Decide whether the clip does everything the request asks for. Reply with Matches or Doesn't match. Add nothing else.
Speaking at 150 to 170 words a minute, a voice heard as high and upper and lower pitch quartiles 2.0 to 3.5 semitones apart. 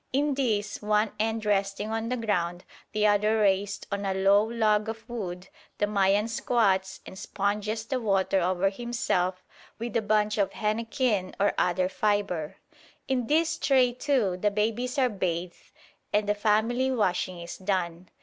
Matches